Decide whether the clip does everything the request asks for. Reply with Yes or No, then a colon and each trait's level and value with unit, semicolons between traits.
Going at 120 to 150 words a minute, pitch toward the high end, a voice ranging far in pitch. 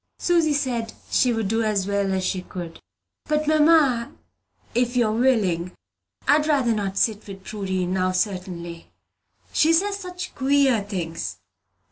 Yes: average, 145 wpm; high, 220 Hz; wide, 7.0 semitones